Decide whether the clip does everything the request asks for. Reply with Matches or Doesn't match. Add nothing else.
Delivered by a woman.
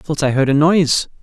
Doesn't match